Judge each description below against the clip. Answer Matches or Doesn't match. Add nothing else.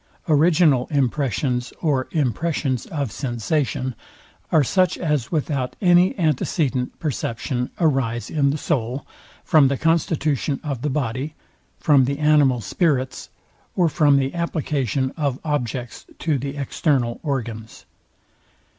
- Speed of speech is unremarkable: Doesn't match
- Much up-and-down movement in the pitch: Doesn't match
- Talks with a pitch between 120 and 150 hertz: Matches